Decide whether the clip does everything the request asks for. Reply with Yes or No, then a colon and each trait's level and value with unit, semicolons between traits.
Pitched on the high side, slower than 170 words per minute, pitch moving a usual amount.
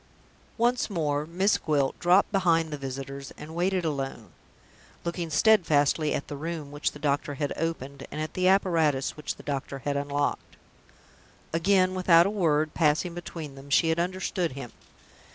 No: medium, 155 Hz; average, 160 wpm; average, 3.7 semitones